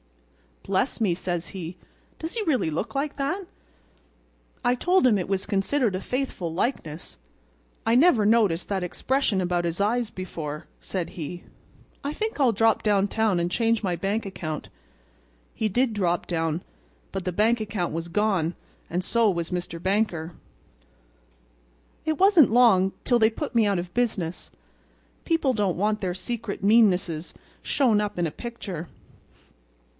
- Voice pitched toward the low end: No, high, 205 Hz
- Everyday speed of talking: Yes, average, 150 wpm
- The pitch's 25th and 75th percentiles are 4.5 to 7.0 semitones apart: Yes, average, 5.0 semitones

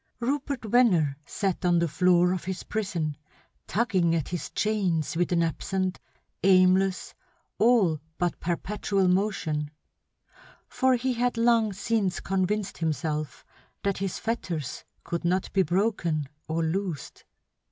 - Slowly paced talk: Yes, slow, 125 wpm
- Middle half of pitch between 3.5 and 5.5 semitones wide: Yes, average, 3.9 semitones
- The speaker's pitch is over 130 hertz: Yes, medium, 185 Hz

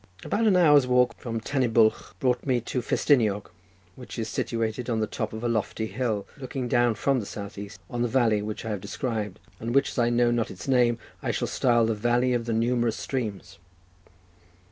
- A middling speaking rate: No, fast, 210 wpm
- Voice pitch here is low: Yes, low, 120 Hz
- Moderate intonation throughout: No, narrow, 2.3 semitones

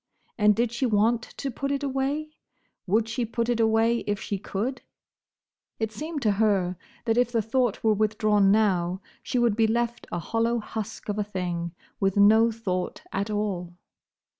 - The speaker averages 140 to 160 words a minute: No, average, 175 wpm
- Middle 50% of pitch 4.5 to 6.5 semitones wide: No, average, 2.8 semitones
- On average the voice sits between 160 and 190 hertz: No, high, 220 Hz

